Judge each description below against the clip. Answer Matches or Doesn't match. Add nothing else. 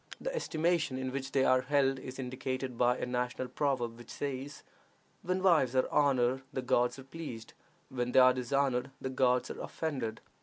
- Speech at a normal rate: Matches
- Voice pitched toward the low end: Matches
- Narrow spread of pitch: Matches